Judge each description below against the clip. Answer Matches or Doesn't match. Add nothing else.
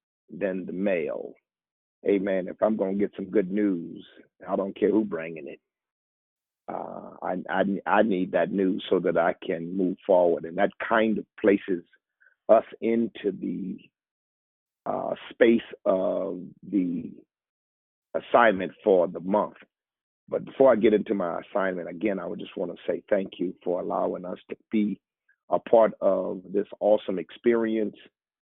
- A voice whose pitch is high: Doesn't match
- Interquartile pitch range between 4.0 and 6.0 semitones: Doesn't match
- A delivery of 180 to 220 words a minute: Doesn't match